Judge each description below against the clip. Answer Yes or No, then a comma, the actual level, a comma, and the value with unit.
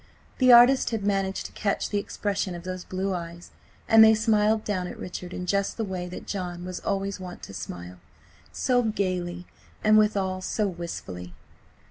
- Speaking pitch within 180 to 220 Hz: Yes, high, 190 Hz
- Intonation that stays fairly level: No, average, 3.0 semitones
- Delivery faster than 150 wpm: Yes, average, 170 wpm